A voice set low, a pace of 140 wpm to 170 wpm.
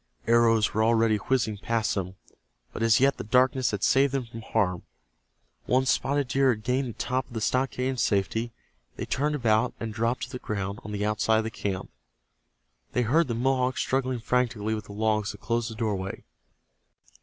No: low, 115 Hz; average, 190 wpm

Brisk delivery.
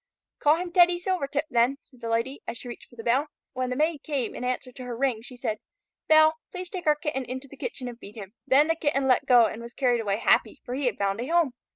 Yes: fast, 265 wpm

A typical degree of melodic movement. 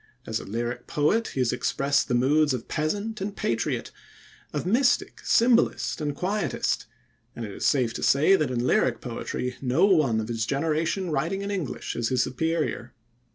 No: wide, 7.0 semitones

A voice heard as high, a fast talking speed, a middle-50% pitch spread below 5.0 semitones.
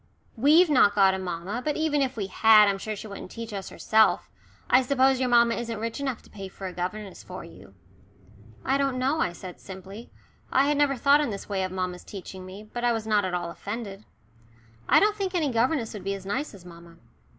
No: high, 215 Hz; fast, 230 wpm; wide, 5.5 semitones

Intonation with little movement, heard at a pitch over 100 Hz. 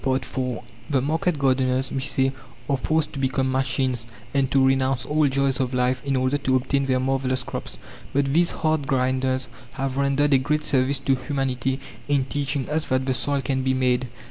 Yes: narrow, 1.3 semitones; low, 135 Hz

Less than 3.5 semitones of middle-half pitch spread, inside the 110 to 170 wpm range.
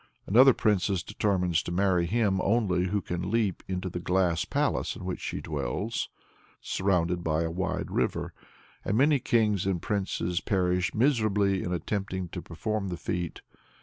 Yes: average, 2.9 semitones; average, 155 wpm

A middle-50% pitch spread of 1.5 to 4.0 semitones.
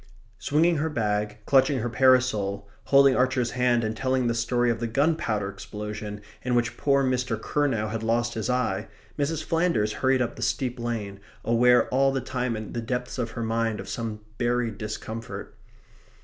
Yes: average, 2.7 semitones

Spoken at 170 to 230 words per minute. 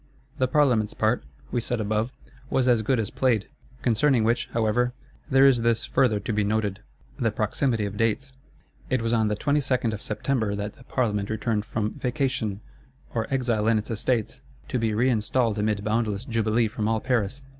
Yes: average, 175 wpm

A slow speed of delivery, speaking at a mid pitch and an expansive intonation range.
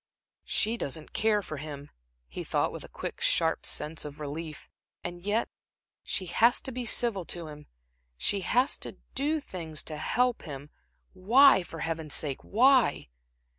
No: average, 160 wpm; medium, 175 Hz; wide, 7.5 semitones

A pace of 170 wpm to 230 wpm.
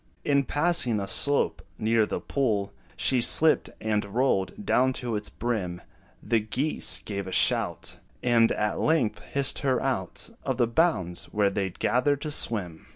No: average, 160 wpm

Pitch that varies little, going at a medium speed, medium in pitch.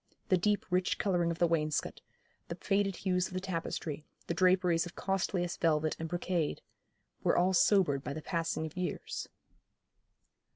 Yes: narrow, 2.1 semitones; average, 160 wpm; medium, 175 Hz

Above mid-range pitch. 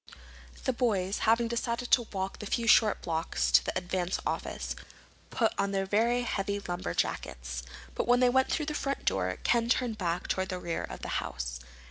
Yes: high, 205 Hz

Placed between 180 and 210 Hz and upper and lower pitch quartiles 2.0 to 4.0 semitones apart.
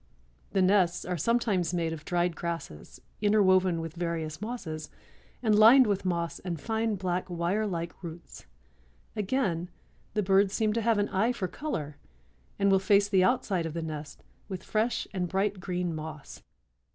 Yes: medium, 185 Hz; average, 3.6 semitones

